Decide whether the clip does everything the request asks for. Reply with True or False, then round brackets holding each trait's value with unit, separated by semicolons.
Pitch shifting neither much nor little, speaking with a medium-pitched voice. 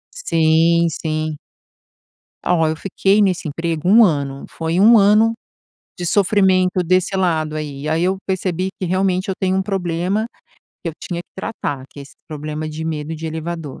True (3.3 semitones; 170 Hz)